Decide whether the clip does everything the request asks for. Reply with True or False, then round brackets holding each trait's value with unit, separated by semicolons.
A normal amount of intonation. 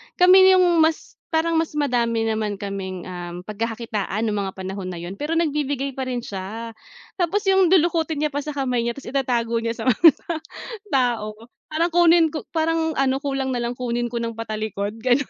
False (6.6 semitones)